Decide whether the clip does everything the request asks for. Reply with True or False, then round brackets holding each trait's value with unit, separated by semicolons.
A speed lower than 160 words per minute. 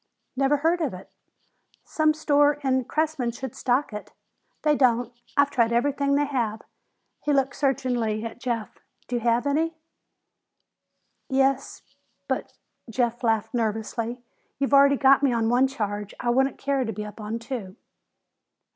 True (150 wpm)